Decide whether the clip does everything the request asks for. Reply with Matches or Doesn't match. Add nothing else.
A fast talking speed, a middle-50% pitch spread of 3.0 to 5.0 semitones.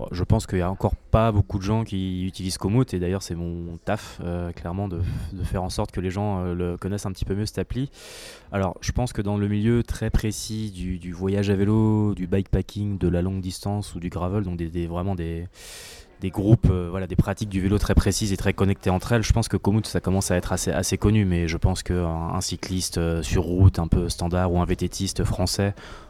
Doesn't match